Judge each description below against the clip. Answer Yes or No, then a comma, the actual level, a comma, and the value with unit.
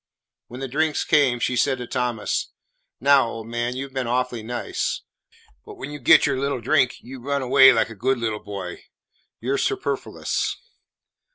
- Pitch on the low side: Yes, low, 125 Hz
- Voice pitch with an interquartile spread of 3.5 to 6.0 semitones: No, narrow, 2.5 semitones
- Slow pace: No, average, 180 wpm